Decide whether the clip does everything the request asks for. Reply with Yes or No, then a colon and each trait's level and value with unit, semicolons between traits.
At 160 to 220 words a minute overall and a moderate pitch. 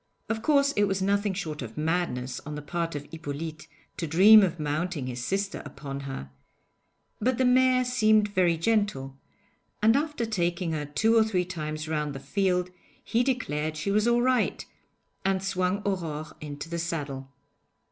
Yes: average, 165 wpm; medium, 175 Hz